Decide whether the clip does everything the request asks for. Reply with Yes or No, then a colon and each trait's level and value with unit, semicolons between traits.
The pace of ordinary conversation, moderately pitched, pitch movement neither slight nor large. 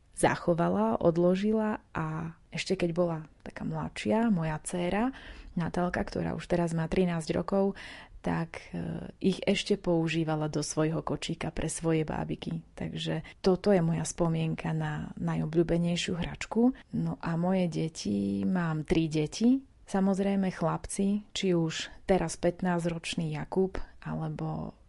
Yes: average, 120 wpm; medium, 170 Hz; average, 3.1 semitones